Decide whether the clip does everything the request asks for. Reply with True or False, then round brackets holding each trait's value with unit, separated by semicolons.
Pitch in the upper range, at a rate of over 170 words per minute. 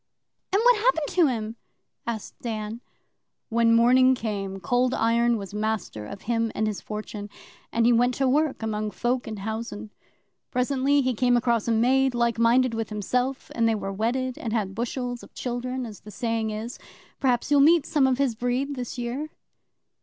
True (235 Hz; 180 wpm)